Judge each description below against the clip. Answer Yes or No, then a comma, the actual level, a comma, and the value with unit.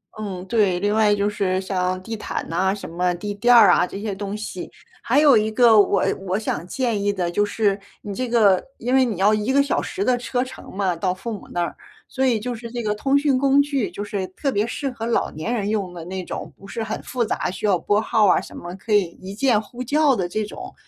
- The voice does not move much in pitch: No, average, 3.9 semitones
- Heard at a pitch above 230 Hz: No, high, 210 Hz